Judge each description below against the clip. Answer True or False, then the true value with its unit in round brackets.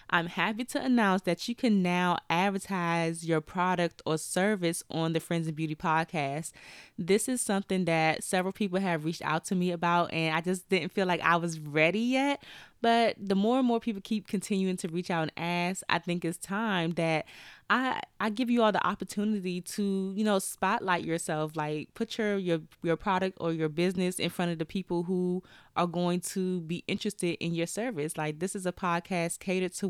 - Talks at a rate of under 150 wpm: False (205 wpm)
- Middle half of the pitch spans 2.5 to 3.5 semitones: True (2.9 semitones)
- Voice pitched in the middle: True (180 Hz)